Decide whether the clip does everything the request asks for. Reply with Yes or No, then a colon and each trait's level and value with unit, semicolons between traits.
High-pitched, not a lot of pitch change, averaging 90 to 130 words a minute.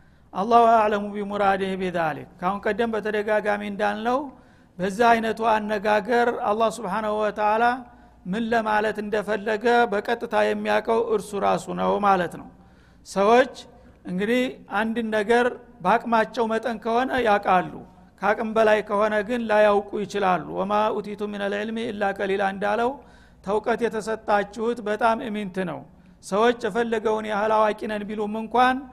Yes: high, 215 Hz; narrow, 2.1 semitones; fast, 110 wpm